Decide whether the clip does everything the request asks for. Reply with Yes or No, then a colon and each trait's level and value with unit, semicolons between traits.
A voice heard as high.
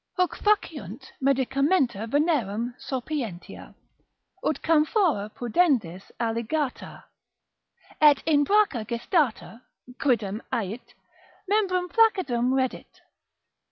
Yes: very high, 270 Hz